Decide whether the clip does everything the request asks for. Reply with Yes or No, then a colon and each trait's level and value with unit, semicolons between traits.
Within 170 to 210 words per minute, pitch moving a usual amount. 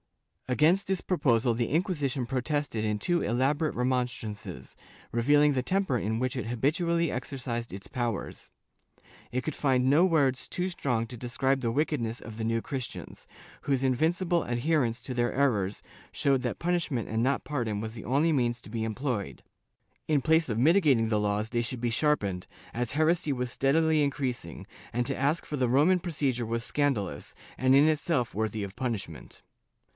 Yes: average, 175 wpm; average, 4.4 semitones